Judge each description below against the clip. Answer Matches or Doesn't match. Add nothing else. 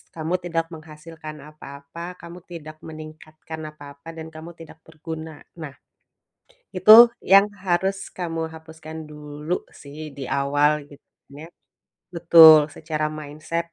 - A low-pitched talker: Doesn't match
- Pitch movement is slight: Matches